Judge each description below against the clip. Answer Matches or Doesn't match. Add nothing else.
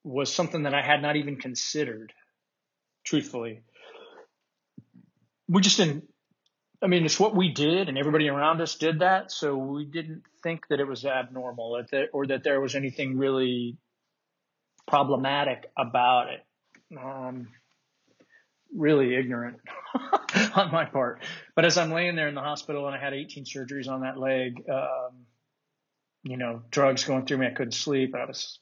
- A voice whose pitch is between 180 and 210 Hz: Doesn't match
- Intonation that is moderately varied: Matches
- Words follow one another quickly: Doesn't match